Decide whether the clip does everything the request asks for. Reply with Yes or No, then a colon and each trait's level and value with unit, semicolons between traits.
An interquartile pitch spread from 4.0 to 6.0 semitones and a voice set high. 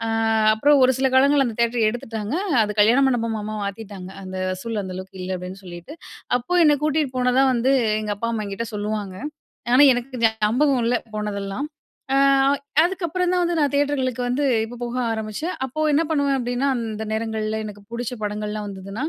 Yes: average, 4.3 semitones; high, 230 Hz